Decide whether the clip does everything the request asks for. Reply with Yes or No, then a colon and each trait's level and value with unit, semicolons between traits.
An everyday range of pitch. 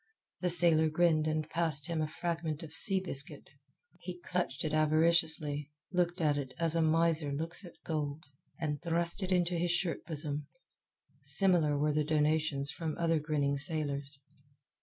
No: narrow, 2.2 semitones